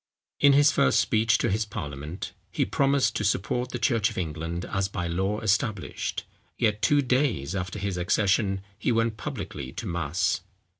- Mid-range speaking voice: No, low, 100 Hz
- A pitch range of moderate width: Yes, average, 4.3 semitones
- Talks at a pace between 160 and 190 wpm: Yes, average, 165 wpm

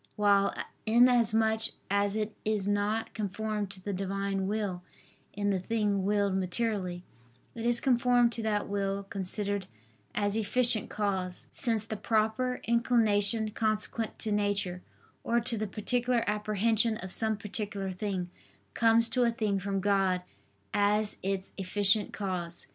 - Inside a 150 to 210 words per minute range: No, slow, 135 wpm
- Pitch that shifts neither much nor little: No, narrow, 2.1 semitones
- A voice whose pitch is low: No, high, 210 Hz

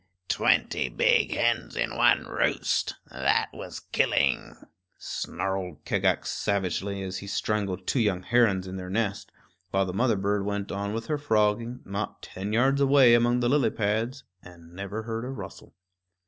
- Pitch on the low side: Yes, low, 105 Hz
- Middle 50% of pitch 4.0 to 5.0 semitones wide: No, average, 3.6 semitones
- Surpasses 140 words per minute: Yes, average, 160 wpm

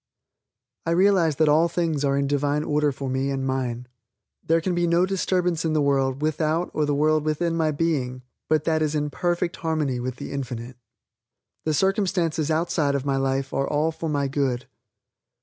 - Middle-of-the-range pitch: Yes, medium, 150 Hz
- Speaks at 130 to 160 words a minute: No, average, 185 wpm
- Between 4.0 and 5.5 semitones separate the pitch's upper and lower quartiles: No, average, 3.2 semitones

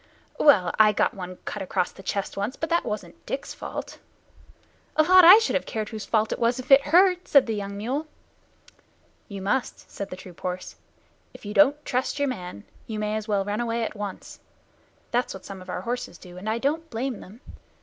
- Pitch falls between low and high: No, high, 220 Hz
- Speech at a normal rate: No, fast, 215 wpm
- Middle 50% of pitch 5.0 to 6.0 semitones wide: Yes, wide, 5.5 semitones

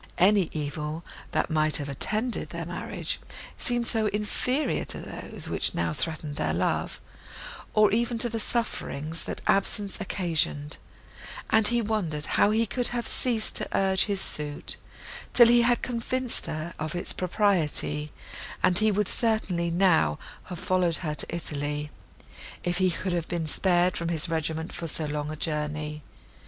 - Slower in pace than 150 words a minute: No, average, 160 wpm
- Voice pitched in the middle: Yes, medium, 175 Hz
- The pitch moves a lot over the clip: Yes, wide, 5.8 semitones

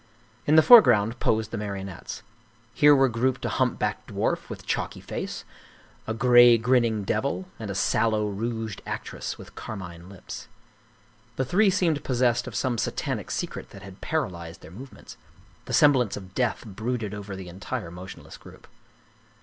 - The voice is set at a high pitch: No, low, 110 Hz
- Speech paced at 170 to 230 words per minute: No, average, 155 wpm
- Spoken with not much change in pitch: No, average, 4.4 semitones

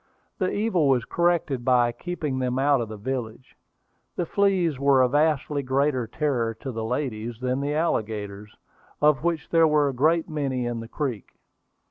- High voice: No, low, 135 Hz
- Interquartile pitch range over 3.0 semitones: Yes, average, 4.1 semitones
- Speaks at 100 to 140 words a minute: No, average, 170 wpm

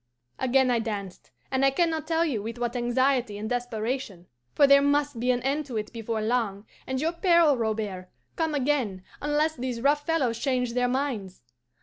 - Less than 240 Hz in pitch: No, very high, 250 Hz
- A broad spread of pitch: No, average, 4.2 semitones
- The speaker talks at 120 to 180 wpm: No, average, 190 wpm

